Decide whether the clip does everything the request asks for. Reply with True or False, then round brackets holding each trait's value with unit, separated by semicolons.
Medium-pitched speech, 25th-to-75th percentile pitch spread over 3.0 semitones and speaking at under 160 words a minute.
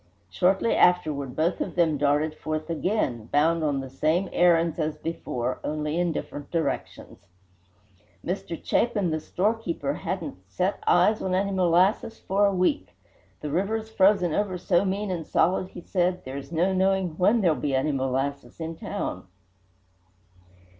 True (170 Hz; 3.9 semitones; 150 wpm)